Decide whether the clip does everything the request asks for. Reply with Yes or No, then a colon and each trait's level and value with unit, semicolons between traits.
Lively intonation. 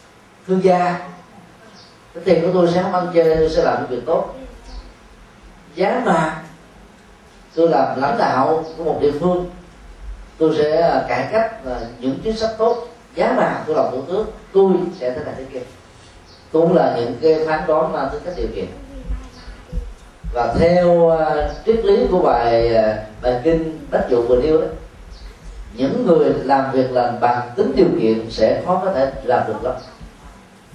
Yes: wide, 6.6 semitones